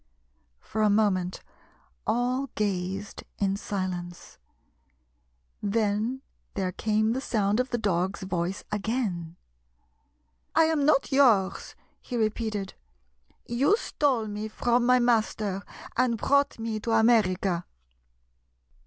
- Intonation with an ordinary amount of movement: Yes, average, 3.9 semitones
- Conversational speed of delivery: No, slow, 110 wpm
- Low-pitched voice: No, high, 215 Hz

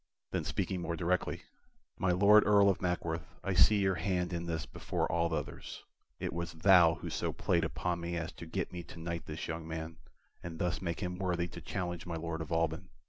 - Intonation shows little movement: Yes, narrow, 1.6 semitones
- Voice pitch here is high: No, very low, 85 Hz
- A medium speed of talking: No, fast, 210 wpm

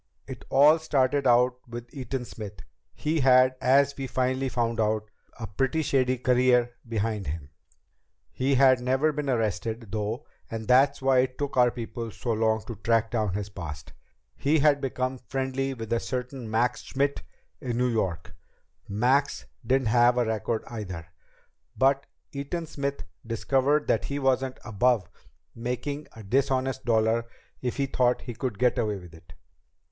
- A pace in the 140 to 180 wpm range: Yes, average, 160 wpm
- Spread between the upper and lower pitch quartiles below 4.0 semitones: Yes, average, 3.1 semitones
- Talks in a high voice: No, low, 125 Hz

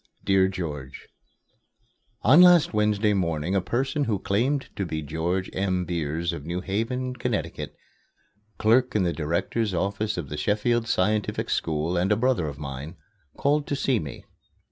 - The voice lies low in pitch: Yes, very low, 95 Hz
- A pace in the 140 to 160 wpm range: Yes, average, 155 wpm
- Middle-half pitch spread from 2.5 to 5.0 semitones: No, wide, 5.5 semitones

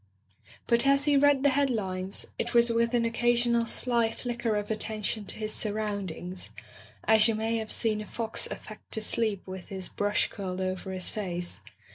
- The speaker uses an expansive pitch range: No, average, 3.0 semitones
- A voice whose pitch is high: Yes, high, 220 Hz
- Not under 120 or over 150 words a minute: No, average, 175 wpm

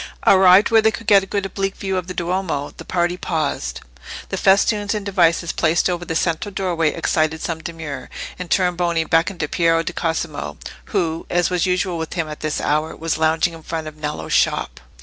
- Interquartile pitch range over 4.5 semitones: No, average, 2.7 semitones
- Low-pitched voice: No, medium, 170 Hz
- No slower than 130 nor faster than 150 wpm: No, average, 200 wpm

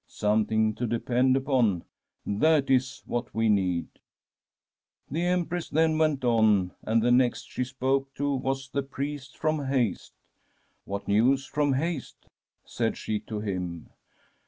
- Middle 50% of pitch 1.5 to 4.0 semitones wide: No, average, 4.4 semitones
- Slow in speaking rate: No, average, 150 wpm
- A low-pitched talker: Yes, low, 130 Hz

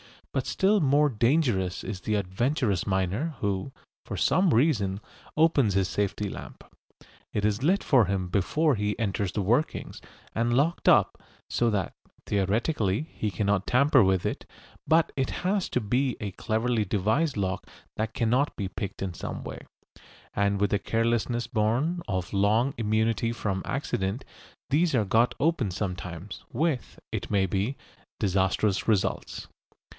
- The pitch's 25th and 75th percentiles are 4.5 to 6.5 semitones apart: Yes, average, 5.2 semitones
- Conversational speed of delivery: Yes, average, 150 wpm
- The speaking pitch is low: Yes, low, 110 Hz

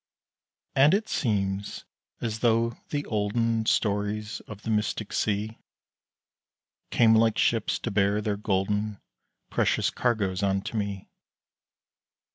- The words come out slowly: Yes, slow, 110 wpm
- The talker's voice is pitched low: Yes, low, 105 Hz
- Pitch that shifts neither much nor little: No, narrow, 2.0 semitones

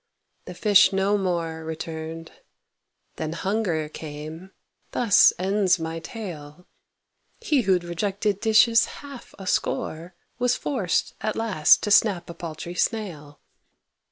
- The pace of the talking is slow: Yes, slow, 120 wpm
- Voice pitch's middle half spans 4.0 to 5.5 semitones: Yes, average, 4.5 semitones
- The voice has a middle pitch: Yes, medium, 180 Hz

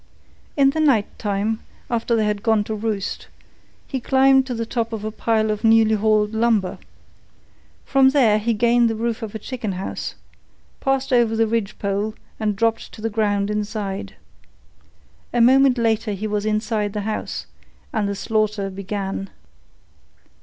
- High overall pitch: Yes, high, 220 Hz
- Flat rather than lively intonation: Yes, narrow, 2.0 semitones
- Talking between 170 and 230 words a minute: No, average, 160 wpm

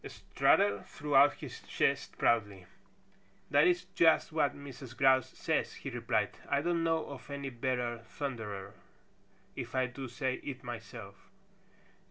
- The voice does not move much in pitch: No, average, 3.4 semitones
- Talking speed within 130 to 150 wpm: Yes, average, 140 wpm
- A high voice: No, low, 130 Hz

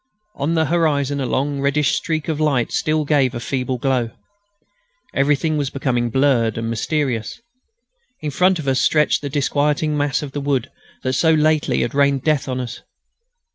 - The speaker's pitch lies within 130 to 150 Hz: Yes, medium, 140 Hz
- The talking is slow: No, average, 175 wpm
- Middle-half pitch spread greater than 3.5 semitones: No, narrow, 2.5 semitones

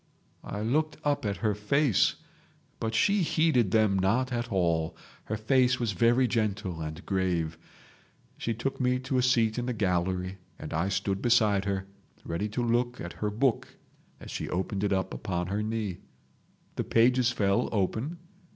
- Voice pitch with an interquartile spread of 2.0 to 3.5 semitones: No, average, 4.4 semitones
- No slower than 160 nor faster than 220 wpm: Yes, average, 165 wpm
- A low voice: Yes, low, 110 Hz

